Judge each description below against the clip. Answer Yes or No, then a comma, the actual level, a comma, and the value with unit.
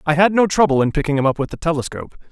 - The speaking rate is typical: No, fast, 285 wpm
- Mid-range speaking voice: Yes, medium, 160 Hz